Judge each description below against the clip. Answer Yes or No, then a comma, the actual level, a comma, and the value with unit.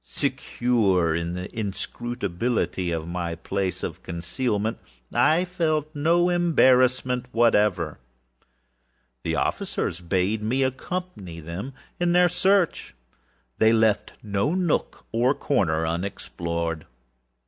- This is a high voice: No, low, 110 Hz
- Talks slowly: Yes, slow, 105 wpm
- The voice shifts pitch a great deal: Yes, wide, 7.6 semitones